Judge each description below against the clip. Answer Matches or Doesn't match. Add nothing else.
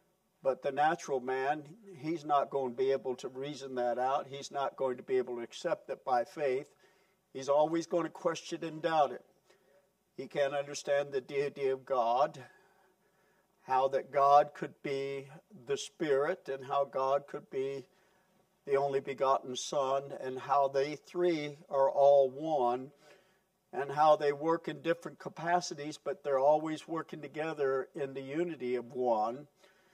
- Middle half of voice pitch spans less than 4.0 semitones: Doesn't match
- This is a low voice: Doesn't match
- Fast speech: Doesn't match